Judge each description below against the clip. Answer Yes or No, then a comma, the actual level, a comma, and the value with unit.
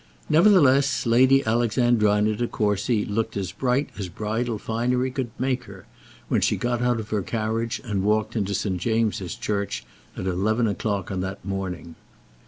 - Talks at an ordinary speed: Yes, average, 160 wpm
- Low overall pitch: Yes, low, 110 Hz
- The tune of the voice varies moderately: Yes, average, 3.3 semitones